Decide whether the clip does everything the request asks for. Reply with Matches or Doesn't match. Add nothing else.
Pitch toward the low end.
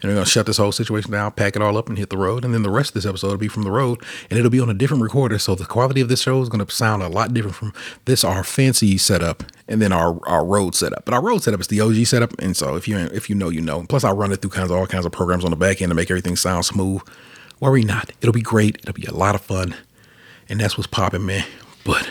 Matches